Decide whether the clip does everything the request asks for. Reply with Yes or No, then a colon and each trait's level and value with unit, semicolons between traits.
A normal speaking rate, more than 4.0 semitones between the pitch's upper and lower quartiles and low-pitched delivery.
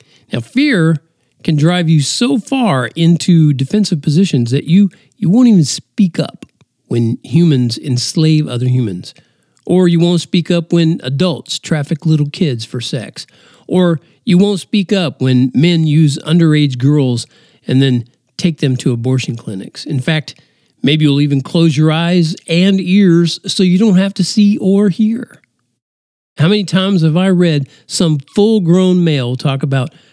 No: average, 160 wpm; average, 4.7 semitones; medium, 165 Hz